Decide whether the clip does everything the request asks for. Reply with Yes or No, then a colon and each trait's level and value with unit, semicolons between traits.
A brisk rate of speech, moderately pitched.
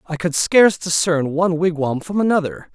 No: average, 175 wpm; medium, 165 Hz